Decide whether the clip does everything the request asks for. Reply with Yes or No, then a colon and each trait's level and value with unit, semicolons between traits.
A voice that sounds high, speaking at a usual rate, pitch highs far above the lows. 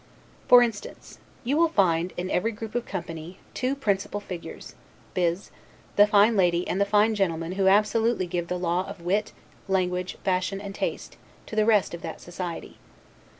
No: high, 195 Hz; average, 170 wpm; average, 3.0 semitones